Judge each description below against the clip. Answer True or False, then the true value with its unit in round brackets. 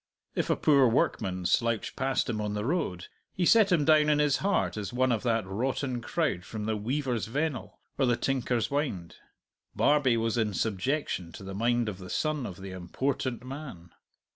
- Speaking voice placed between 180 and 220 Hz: False (120 Hz)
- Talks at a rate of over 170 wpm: True (190 wpm)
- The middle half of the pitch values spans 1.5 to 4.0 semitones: False (5.4 semitones)